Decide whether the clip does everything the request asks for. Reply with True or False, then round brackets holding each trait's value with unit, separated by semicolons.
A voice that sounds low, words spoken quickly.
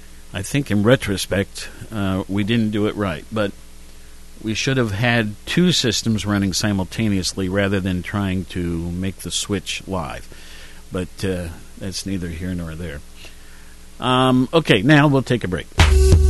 False (95 Hz; 150 wpm)